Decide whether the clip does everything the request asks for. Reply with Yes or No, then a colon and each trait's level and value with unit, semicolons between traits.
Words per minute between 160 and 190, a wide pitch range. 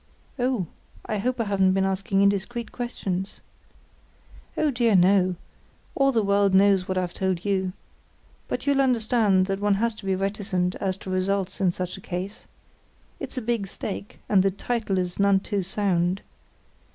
No: average, 165 wpm; narrow, 2.5 semitones